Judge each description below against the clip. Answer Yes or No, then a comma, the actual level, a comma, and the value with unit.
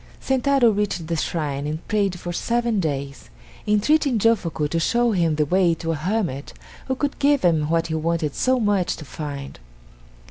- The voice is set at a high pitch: No, medium, 175 Hz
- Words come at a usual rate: Yes, average, 175 wpm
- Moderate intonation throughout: No, wide, 6.5 semitones